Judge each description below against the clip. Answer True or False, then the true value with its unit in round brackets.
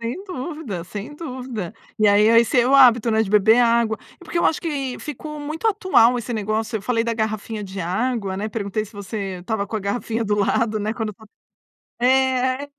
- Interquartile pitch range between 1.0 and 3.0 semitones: False (3.5 semitones)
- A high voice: True (230 Hz)